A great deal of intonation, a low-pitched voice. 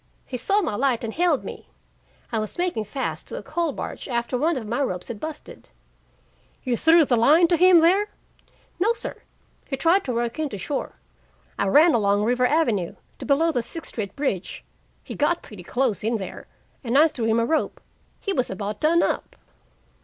No: wide, 6.4 semitones; very high, 260 Hz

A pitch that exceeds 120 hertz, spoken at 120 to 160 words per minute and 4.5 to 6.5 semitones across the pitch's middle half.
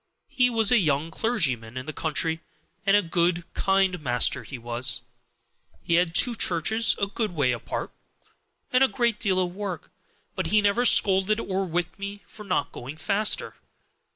No: medium, 185 Hz; average, 170 wpm; average, 4.9 semitones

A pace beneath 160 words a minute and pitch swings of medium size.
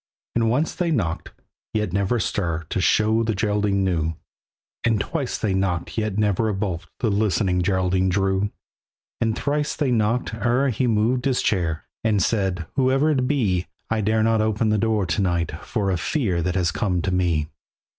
No: average, 185 wpm; average, 3.8 semitones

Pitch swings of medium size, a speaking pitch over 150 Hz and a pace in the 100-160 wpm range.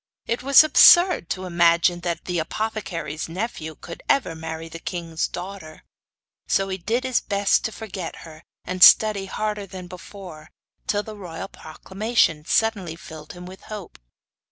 Yes: average, 4.2 semitones; medium, 185 Hz; average, 155 wpm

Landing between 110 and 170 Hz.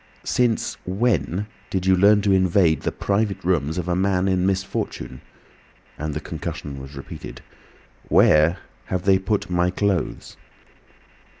No: very low, 95 Hz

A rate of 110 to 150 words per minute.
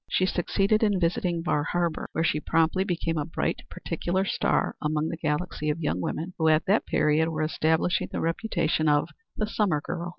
No: average, 190 wpm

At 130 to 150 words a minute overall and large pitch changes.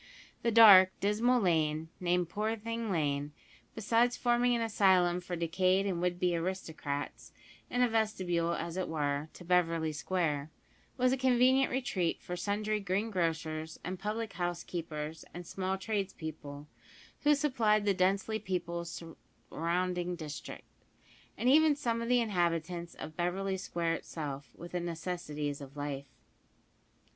No: average, 140 wpm; average, 4.5 semitones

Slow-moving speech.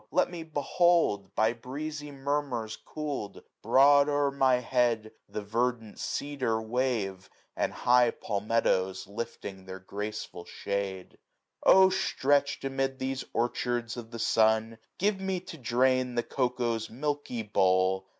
Yes: slow, 130 wpm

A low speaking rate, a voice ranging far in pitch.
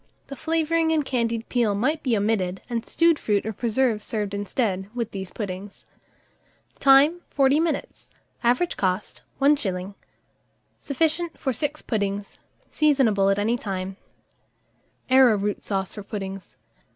Yes: slow, 125 wpm; wide, 5.8 semitones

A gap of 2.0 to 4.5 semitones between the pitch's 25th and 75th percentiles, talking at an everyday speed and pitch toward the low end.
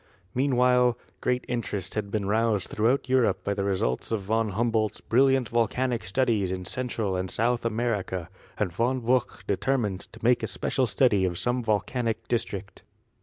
Yes: average, 3.6 semitones; average, 165 wpm; low, 115 Hz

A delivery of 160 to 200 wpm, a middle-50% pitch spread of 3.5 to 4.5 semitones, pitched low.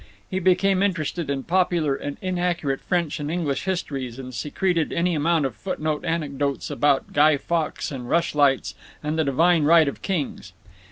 No: average, 165 wpm; average, 3.8 semitones; medium, 155 Hz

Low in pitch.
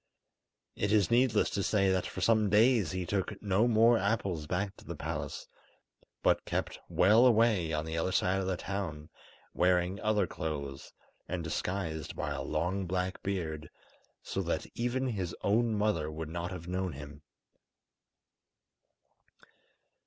Yes: very low, 95 Hz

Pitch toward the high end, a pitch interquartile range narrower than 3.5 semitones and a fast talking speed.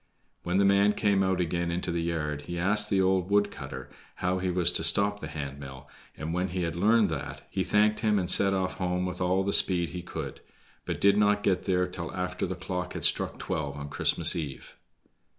No: very low, 90 Hz; narrow, 2.6 semitones; fast, 220 wpm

